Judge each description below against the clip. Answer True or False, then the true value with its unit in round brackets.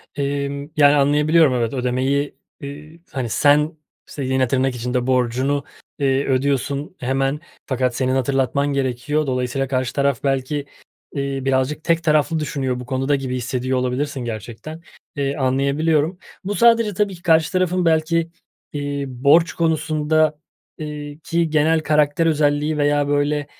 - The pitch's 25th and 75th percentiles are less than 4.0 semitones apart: True (2.7 semitones)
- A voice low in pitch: False (145 Hz)